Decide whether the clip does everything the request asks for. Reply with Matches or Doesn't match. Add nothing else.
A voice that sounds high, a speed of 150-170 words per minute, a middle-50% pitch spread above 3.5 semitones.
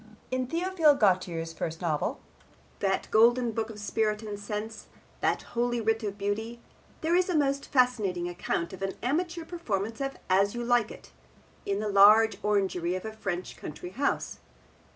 Matches